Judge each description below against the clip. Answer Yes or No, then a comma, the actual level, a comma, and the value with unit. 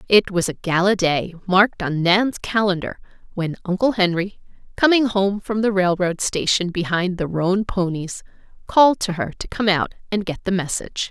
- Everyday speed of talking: Yes, average, 175 wpm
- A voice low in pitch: No, high, 190 Hz